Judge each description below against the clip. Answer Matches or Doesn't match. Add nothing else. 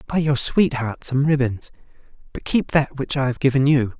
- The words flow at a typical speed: Matches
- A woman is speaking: Doesn't match